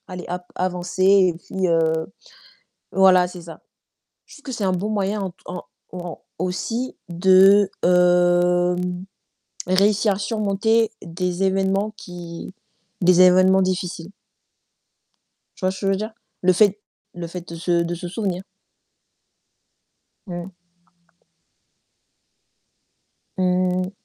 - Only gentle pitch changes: Yes, narrow, 1.7 semitones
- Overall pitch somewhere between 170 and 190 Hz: Yes, medium, 185 Hz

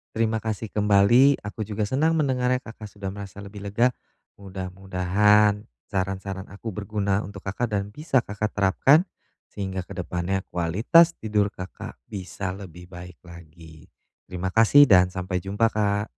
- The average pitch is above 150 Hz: No, low, 100 Hz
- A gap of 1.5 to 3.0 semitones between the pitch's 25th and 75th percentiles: Yes, narrow, 2.6 semitones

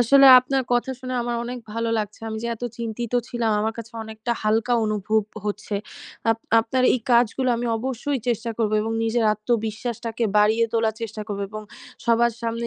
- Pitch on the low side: No, high, 230 Hz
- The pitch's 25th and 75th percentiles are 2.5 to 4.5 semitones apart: No, narrow, 1.7 semitones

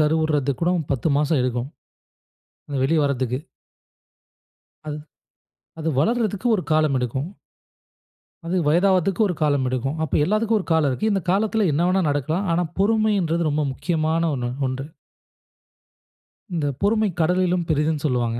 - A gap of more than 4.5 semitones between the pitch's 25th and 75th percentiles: Yes, average, 4.9 semitones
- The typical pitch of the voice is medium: Yes, medium, 160 Hz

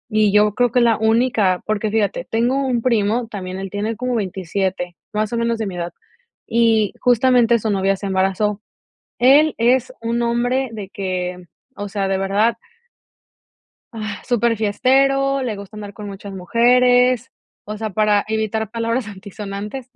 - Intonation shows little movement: No, average, 3.0 semitones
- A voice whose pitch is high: Yes, high, 220 Hz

